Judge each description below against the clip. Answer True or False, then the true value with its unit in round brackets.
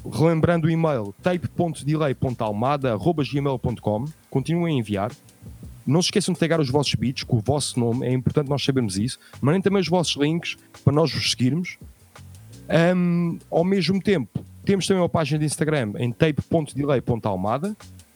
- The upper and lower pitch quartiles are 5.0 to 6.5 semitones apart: True (5.5 semitones)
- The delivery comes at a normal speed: True (150 wpm)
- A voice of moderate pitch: True (145 Hz)